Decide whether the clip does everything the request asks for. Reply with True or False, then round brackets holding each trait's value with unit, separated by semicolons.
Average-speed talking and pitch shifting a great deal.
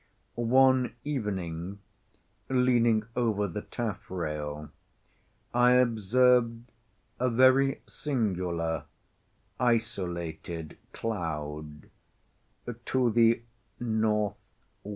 False (65 wpm; 6.2 semitones)